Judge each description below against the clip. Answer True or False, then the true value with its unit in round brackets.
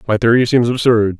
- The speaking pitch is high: False (115 Hz)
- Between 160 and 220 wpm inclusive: True (200 wpm)